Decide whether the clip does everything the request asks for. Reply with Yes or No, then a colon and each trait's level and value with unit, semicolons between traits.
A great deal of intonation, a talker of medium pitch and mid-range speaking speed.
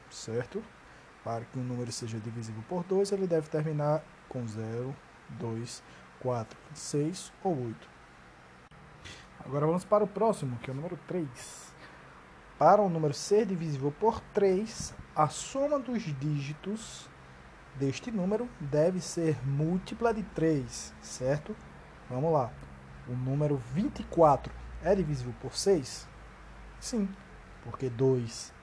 Yes: wide, 7.5 semitones; medium, 145 Hz; average, 130 wpm